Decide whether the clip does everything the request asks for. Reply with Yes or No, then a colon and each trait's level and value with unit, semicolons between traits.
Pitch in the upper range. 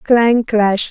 Yes: high, 225 Hz